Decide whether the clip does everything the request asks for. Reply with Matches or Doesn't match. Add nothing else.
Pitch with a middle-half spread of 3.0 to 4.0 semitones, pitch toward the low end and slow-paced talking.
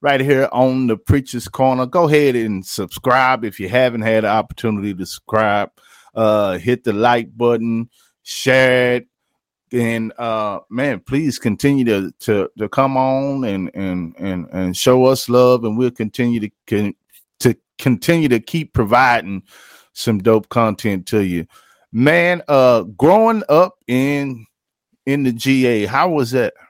Doesn't match